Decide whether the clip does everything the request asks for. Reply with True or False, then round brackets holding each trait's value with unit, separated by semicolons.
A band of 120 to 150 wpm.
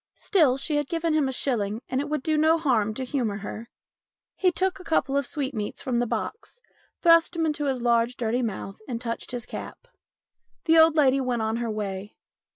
False (205 wpm)